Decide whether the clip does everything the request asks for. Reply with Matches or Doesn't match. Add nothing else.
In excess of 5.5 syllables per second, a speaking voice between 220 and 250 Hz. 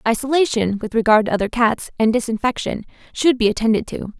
Matches